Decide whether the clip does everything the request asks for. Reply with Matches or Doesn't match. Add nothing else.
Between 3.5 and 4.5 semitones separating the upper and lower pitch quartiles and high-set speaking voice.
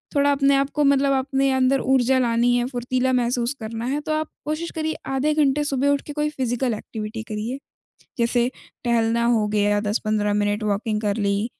Matches